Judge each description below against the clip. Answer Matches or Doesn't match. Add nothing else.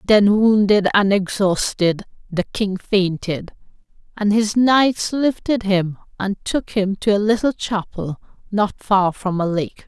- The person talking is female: Matches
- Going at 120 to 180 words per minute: Matches